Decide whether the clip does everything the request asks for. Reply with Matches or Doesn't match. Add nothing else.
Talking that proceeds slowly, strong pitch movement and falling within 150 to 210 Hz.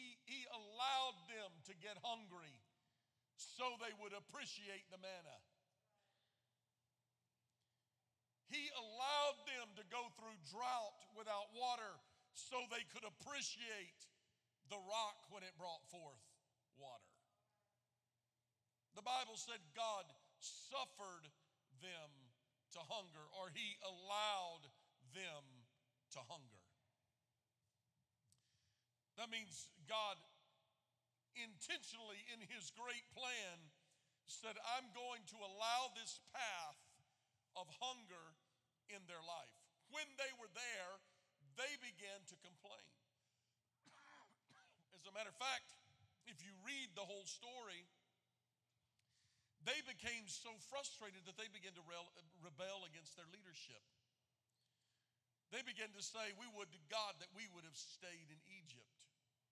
Matches